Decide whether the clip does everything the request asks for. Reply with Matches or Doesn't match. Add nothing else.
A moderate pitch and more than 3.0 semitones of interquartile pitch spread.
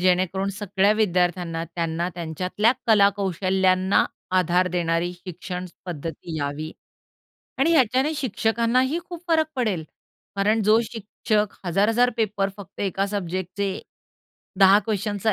Doesn't match